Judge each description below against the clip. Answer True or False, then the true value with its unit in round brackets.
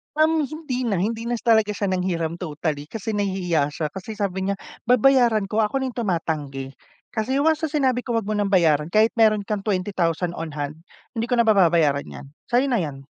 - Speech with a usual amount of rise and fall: False (5.7 semitones)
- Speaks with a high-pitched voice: True (200 Hz)